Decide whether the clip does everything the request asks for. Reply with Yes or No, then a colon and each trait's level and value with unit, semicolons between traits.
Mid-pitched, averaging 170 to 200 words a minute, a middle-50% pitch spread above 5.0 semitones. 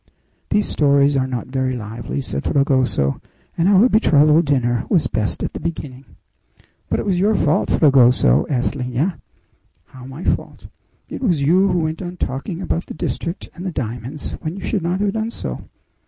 Yes: medium, 145 Hz; average, 180 wpm; wide, 5.6 semitones